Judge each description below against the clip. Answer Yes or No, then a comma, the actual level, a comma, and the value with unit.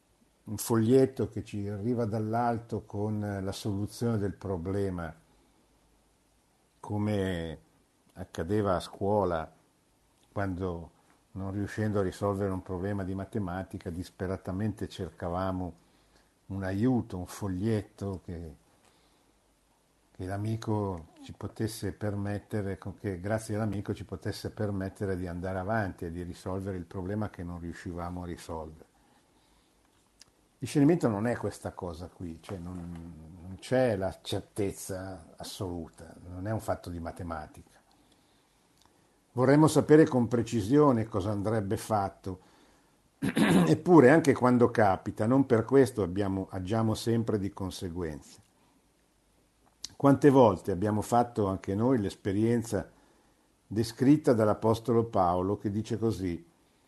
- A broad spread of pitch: No, average, 3.2 semitones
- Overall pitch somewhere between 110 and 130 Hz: No, low, 100 Hz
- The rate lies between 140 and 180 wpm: No, slow, 115 wpm